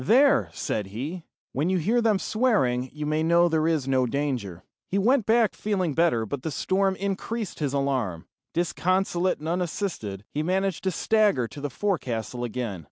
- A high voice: No, medium, 160 Hz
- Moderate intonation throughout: No, wide, 7.1 semitones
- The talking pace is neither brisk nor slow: Yes, average, 170 wpm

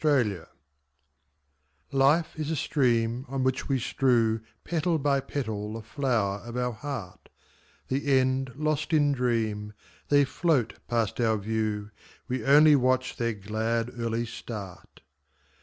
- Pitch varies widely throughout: No, average, 3.8 semitones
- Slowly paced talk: Yes, slow, 130 wpm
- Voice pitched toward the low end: Yes, low, 125 Hz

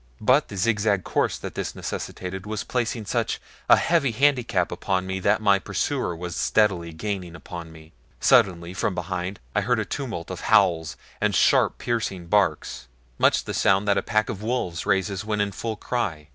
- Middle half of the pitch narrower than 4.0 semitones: Yes, average, 3.5 semitones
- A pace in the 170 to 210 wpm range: Yes, average, 180 wpm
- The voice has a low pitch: Yes, low, 100 Hz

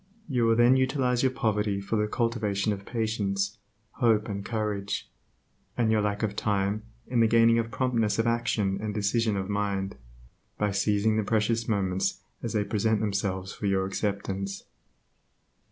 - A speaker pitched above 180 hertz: No, low, 105 Hz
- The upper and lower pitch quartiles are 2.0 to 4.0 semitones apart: Yes, narrow, 2.4 semitones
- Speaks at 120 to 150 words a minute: No, average, 160 wpm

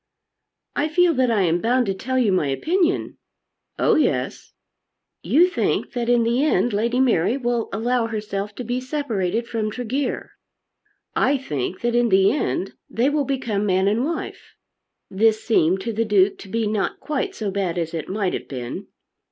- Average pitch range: Yes, average, 4.6 semitones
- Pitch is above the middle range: Yes, high, 230 Hz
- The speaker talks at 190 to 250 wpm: No, average, 175 wpm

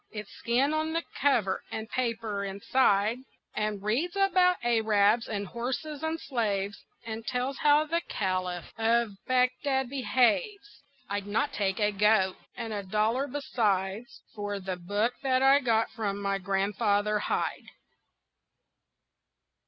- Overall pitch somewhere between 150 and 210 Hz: No, high, 225 Hz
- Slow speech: Yes, slow, 130 wpm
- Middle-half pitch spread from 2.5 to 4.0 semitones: No, average, 4.7 semitones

